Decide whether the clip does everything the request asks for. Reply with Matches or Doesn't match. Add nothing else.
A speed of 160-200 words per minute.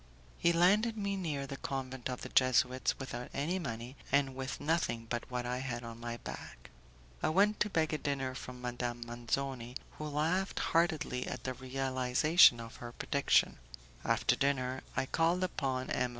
Matches